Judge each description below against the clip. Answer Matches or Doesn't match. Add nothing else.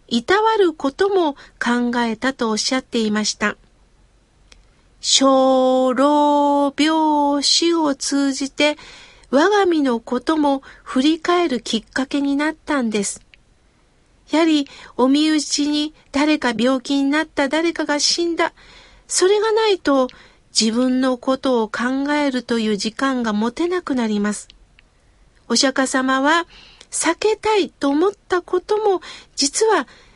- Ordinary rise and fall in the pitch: Matches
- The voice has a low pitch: Doesn't match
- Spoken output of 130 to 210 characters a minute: Matches